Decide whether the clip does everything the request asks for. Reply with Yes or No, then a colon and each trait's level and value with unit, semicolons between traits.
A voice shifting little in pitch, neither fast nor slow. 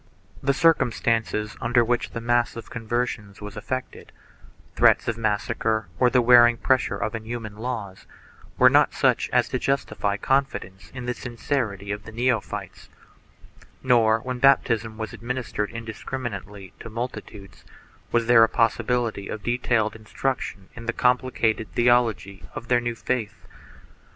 Yes: narrow, 2.3 semitones; average, 145 wpm